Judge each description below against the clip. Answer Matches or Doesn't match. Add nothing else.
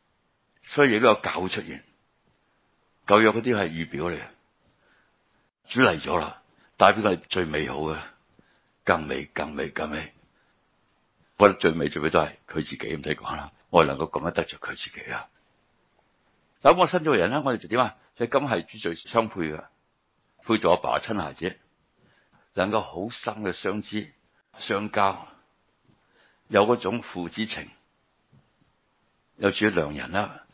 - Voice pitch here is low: Matches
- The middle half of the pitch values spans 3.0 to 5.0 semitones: Matches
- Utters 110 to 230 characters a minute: Matches